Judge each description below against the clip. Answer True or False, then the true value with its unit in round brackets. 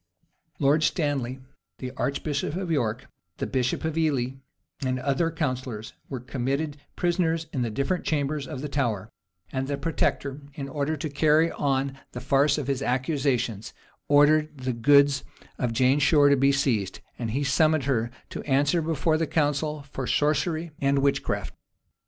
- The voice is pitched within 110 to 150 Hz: True (140 Hz)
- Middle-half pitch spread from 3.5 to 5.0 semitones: False (2.7 semitones)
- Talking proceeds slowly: False (155 wpm)